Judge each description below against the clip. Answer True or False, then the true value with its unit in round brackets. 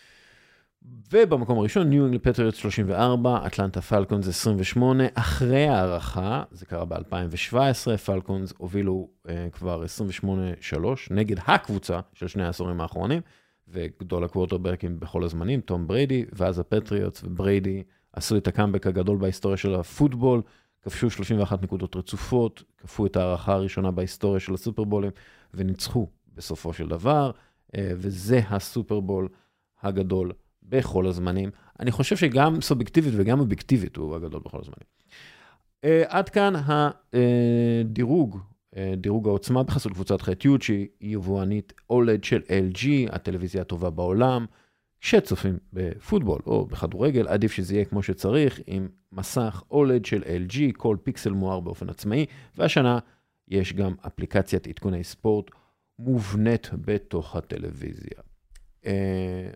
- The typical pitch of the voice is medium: False (100 Hz)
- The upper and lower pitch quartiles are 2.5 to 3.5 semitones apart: False (4.5 semitones)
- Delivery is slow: True (120 wpm)